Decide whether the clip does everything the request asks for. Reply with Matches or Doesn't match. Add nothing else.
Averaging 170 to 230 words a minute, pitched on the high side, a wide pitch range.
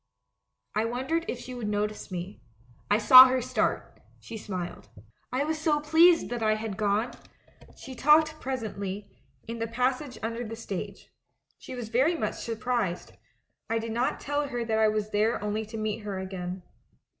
Doesn't match